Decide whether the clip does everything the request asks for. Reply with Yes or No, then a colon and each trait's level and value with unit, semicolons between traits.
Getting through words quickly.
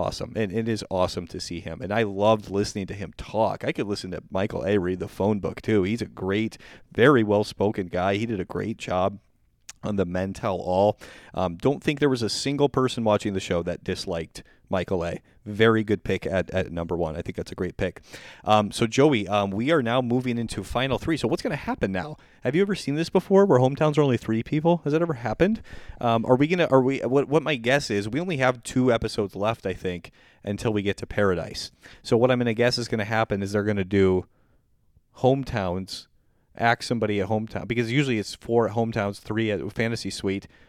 Yes: fast, 225 wpm